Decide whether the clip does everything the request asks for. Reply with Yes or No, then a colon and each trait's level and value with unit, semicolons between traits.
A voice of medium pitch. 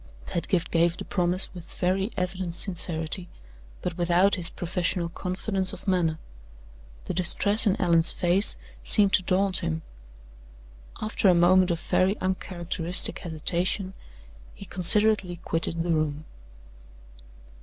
Yes: medium, 180 Hz